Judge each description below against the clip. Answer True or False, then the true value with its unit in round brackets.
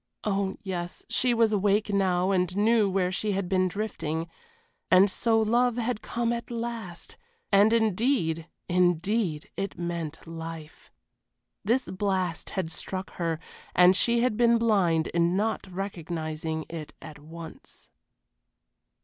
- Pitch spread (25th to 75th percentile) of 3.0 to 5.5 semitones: True (4.4 semitones)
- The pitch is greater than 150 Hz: True (190 Hz)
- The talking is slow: True (130 wpm)